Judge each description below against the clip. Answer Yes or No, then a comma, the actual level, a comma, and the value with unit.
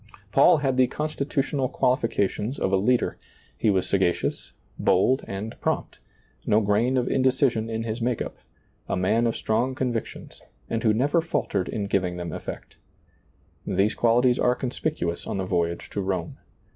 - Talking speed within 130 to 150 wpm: No, average, 160 wpm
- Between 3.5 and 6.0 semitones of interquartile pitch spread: Yes, average, 4.6 semitones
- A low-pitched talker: Yes, low, 115 Hz